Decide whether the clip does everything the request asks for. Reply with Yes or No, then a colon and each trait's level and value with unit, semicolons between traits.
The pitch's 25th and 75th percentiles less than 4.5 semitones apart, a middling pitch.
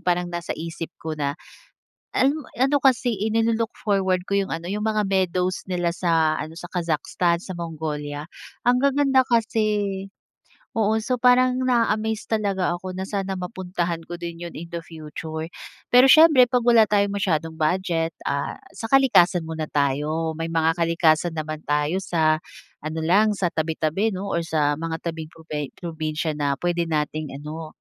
No: average, 4.8 semitones; medium, 175 Hz